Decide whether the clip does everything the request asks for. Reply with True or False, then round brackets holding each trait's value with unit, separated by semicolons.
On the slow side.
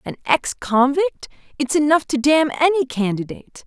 True (130 wpm)